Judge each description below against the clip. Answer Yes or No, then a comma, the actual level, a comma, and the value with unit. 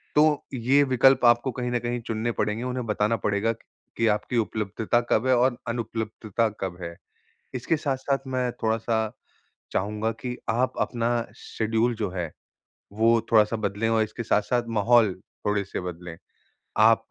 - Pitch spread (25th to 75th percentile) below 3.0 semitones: Yes, narrow, 2.5 semitones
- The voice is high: No, low, 115 Hz